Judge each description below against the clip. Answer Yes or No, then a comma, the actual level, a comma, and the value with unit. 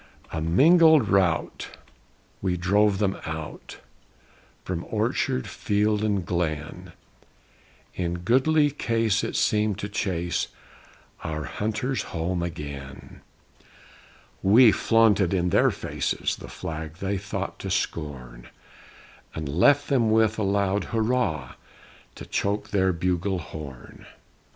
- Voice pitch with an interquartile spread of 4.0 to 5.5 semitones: Yes, average, 4.6 semitones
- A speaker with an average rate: No, slow, 110 wpm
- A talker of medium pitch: No, very low, 95 Hz